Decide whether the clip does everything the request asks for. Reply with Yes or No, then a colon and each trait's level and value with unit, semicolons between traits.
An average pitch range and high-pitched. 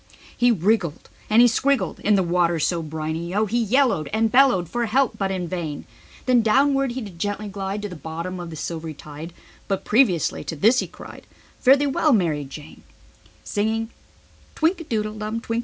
No: wide, 6.2 semitones; high, 195 Hz